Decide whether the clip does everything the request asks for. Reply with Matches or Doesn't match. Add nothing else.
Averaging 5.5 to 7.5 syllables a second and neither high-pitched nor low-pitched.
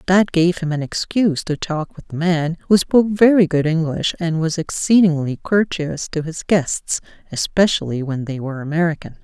Doesn't match